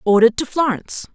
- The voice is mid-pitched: No, high, 240 Hz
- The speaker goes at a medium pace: Yes, average, 155 wpm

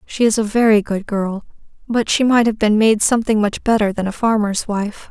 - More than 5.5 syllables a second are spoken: No, 5.3 syllables/s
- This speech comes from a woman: Yes, female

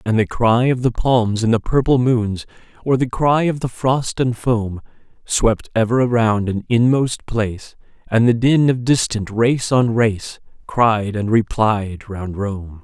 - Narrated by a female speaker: No, male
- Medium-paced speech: Yes, average, 175 wpm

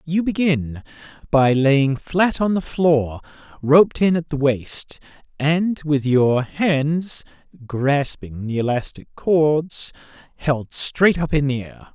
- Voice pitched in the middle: Yes, medium, 145 Hz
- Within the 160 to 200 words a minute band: No, slow, 135 wpm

